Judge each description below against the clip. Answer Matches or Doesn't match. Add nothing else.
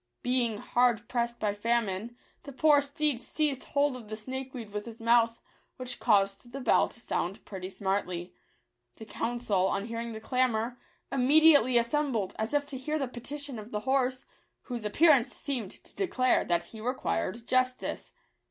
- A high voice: Matches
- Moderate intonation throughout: Matches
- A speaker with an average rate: Matches